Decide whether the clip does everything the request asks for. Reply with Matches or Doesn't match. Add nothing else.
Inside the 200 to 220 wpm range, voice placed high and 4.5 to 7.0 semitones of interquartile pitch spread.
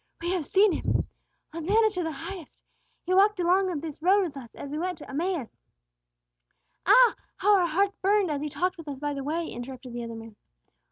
Matches